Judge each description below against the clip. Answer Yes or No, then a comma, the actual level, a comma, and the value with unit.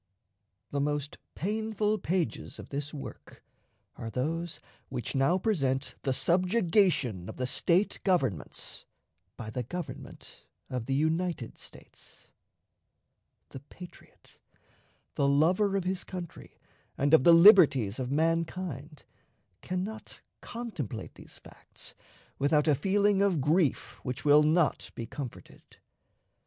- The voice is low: No, medium, 160 Hz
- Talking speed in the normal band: No, slow, 120 wpm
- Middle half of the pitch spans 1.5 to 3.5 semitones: No, average, 5.3 semitones